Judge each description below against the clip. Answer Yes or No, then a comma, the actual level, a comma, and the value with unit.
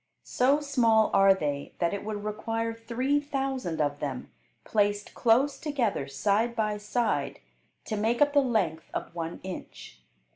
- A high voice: Yes, high, 220 Hz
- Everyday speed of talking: Yes, average, 150 wpm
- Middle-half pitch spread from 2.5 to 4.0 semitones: No, average, 5.0 semitones